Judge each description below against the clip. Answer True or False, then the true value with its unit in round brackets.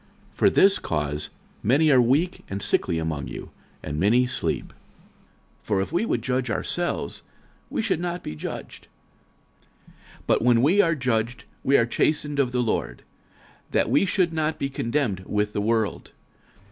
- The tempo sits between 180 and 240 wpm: False (170 wpm)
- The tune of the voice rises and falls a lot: True (7.0 semitones)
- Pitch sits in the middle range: False (125 Hz)